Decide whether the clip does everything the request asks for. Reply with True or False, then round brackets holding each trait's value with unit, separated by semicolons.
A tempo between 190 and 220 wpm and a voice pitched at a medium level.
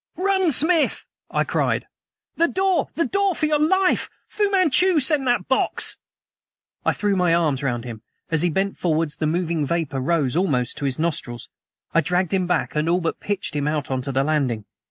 True (195 wpm; 170 Hz)